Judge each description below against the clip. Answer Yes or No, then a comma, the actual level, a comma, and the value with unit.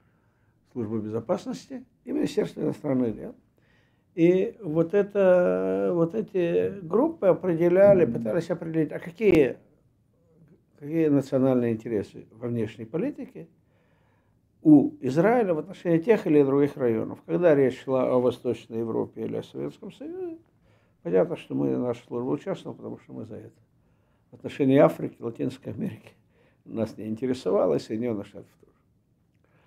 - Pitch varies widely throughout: Yes, wide, 7.2 semitones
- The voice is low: No, medium, 145 Hz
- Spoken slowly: No, average, 130 wpm